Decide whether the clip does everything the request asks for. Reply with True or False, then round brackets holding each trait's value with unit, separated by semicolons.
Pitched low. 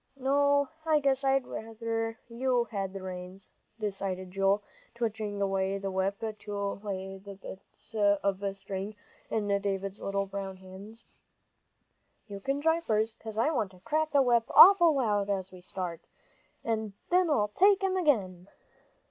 False (205 Hz)